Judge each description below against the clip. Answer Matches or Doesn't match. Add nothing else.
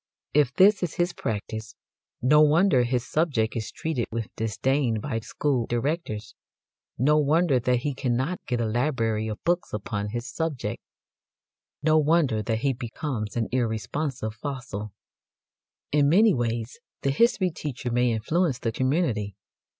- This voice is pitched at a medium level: Doesn't match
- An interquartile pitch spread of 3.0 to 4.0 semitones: Doesn't match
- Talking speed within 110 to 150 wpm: Matches